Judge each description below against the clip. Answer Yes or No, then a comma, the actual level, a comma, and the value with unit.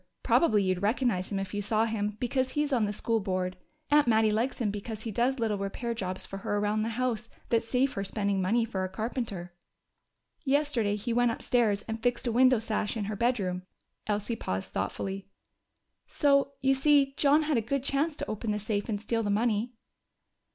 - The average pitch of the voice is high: Yes, high, 225 Hz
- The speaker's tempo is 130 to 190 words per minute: No, average, 200 wpm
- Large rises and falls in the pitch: No, average, 3.4 semitones